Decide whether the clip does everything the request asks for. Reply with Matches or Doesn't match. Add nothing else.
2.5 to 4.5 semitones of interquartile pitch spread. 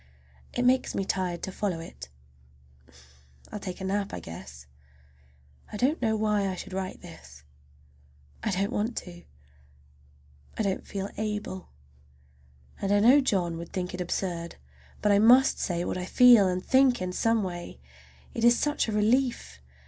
Matches